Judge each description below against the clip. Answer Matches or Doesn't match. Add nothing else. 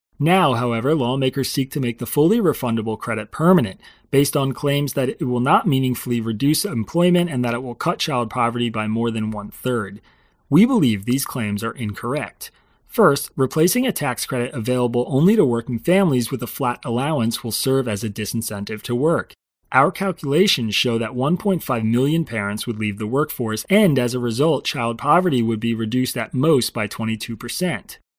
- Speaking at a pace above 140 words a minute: Matches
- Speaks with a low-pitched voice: Matches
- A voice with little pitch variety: Doesn't match